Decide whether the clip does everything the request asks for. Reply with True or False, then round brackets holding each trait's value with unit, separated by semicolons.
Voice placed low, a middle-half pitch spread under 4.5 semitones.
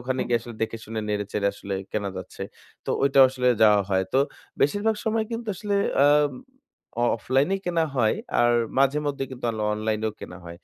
False (125 Hz; 5.4 semitones)